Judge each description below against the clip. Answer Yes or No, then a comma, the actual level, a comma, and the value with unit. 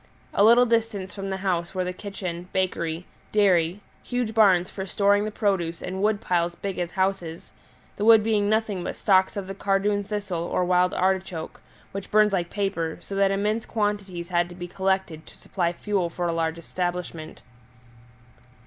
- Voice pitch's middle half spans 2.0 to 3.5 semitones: Yes, narrow, 2.6 semitones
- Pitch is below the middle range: No, high, 190 Hz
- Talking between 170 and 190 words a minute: Yes, average, 175 wpm